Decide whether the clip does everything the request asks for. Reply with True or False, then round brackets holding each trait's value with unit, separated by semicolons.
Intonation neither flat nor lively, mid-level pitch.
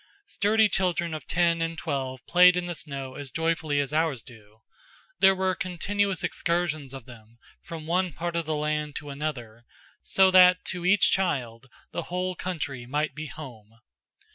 True (4.8 semitones; 160 Hz)